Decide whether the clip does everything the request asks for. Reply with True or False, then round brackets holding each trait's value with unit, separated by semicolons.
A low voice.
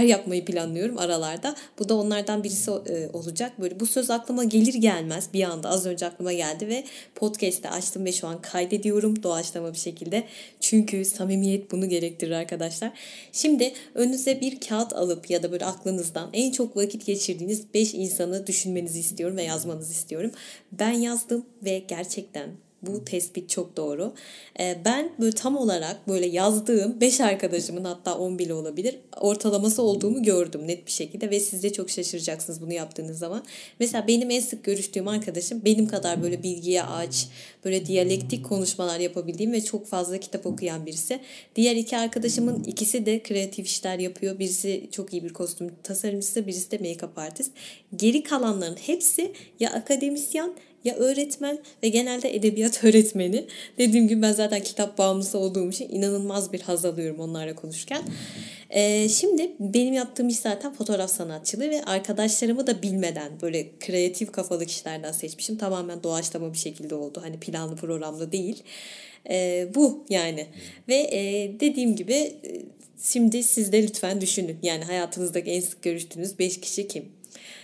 False (195 Hz)